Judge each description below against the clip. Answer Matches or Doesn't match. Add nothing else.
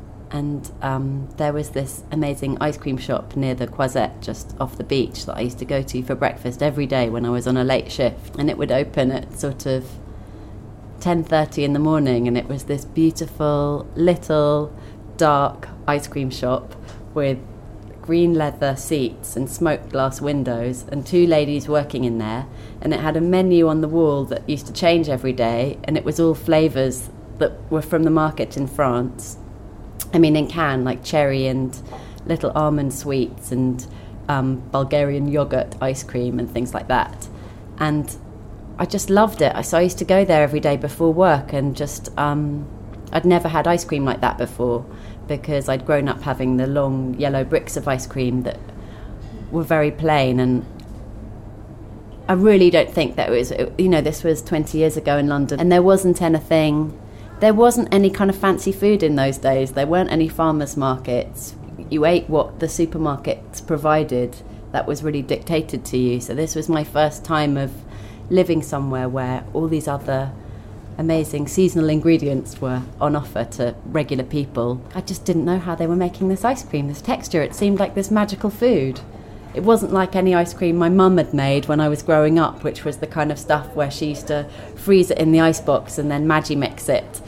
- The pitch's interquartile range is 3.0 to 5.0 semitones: Matches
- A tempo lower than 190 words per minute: Doesn't match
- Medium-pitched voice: Matches